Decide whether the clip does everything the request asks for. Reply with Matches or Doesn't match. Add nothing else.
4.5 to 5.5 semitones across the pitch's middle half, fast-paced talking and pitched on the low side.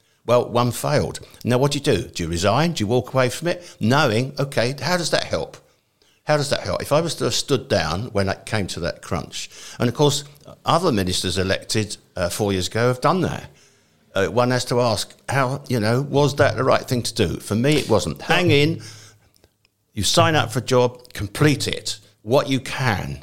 Matches